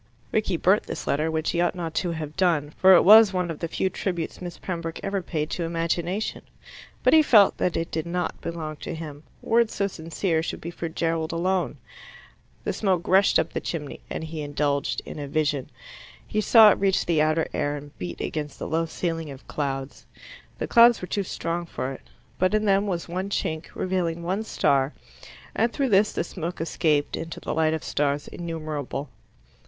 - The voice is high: No, medium, 165 Hz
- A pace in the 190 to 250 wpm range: Yes, average, 200 wpm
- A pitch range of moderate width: Yes, average, 3.3 semitones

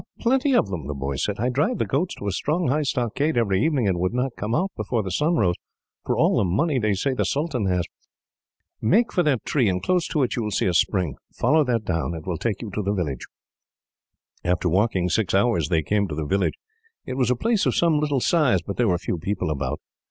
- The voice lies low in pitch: Yes, low, 110 Hz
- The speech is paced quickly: Yes, fast, 245 wpm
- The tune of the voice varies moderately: No, wide, 8.0 semitones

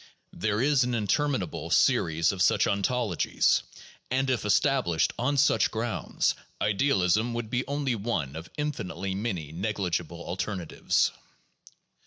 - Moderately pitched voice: No, low, 105 Hz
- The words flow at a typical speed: No, slow, 120 wpm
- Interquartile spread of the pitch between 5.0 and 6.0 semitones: Yes, wide, 5.6 semitones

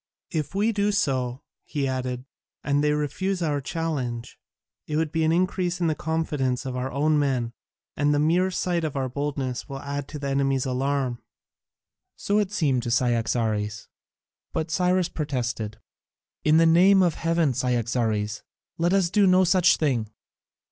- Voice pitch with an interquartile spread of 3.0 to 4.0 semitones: No, average, 4.8 semitones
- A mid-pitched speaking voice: Yes, medium, 145 Hz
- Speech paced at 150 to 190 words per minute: Yes, average, 155 wpm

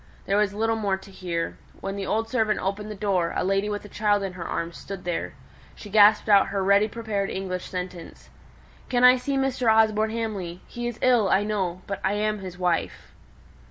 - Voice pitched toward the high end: Yes, high, 205 Hz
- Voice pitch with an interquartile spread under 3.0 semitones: Yes, narrow, 2.5 semitones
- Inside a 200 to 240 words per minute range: Yes, fast, 205 wpm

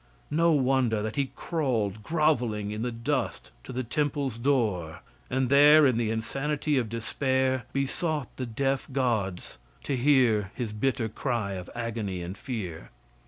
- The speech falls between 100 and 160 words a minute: Yes, average, 150 wpm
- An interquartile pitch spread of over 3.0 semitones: Yes, average, 4.1 semitones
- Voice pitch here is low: Yes, low, 125 Hz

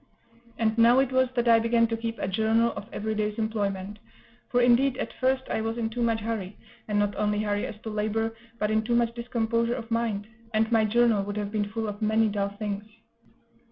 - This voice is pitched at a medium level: No, high, 225 Hz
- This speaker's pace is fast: Yes, fast, 220 wpm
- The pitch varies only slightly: Yes, narrow, 1.9 semitones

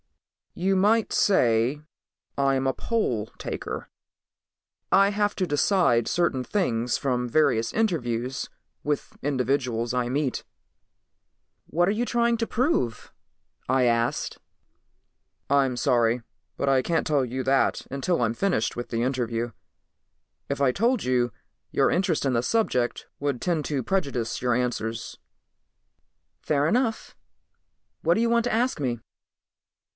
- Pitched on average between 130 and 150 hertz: Yes, low, 135 Hz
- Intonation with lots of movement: Yes, wide, 7.3 semitones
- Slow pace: Yes, slow, 130 wpm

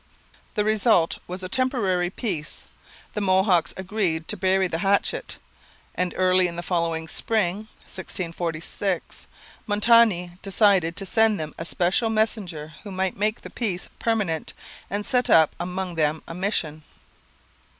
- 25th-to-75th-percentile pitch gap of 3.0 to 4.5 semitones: Yes, average, 3.5 semitones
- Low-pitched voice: No, medium, 185 Hz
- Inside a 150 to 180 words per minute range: No, average, 140 wpm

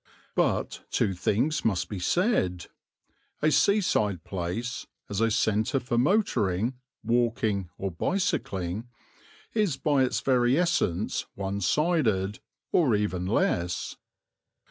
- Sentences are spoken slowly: Yes, slow, 110 wpm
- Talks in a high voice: No, low, 110 Hz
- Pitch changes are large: Yes, wide, 6.5 semitones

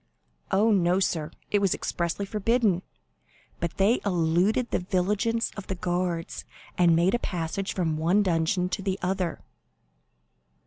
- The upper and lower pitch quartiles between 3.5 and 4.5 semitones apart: No, average, 2.8 semitones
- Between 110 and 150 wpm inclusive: Yes, average, 140 wpm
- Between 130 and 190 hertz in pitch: Yes, medium, 185 Hz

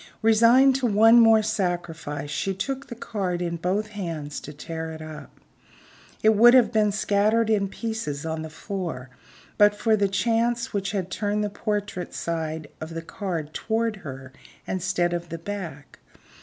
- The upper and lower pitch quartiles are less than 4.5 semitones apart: No, average, 5.0 semitones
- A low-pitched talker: No, high, 195 Hz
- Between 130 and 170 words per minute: Yes, average, 165 wpm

